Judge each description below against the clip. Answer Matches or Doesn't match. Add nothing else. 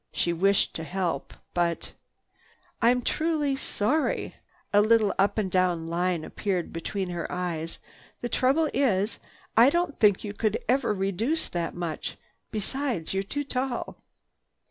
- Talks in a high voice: Matches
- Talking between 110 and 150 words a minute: Matches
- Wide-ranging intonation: Matches